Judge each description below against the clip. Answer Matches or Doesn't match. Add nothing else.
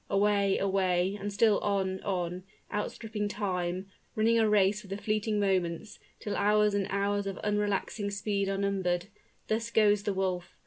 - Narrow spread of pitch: Matches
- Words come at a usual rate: Matches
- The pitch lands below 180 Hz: Doesn't match